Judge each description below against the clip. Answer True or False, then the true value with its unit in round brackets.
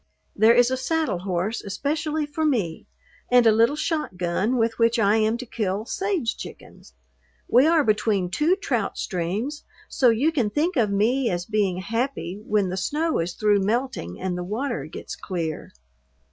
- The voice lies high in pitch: True (225 Hz)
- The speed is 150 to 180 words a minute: True (170 wpm)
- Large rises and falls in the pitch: True (6.3 semitones)